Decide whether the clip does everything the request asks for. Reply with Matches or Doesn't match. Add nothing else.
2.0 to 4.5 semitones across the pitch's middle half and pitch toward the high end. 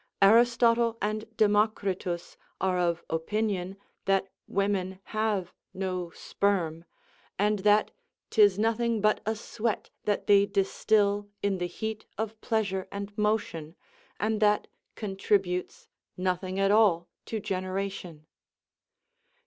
Matches